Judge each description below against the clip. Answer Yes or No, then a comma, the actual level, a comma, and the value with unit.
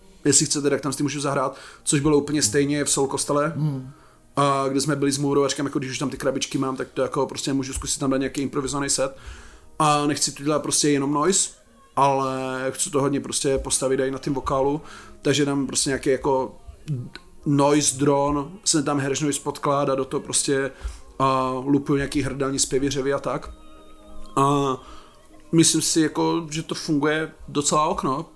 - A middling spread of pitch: No, narrow, 1.7 semitones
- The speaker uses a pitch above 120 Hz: Yes, medium, 140 Hz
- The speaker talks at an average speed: No, fast, 180 wpm